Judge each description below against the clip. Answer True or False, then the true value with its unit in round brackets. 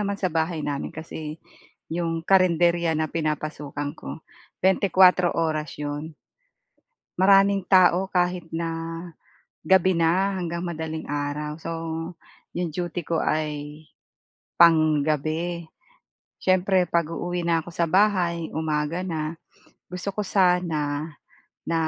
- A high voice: False (165 Hz)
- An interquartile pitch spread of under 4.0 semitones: True (2.5 semitones)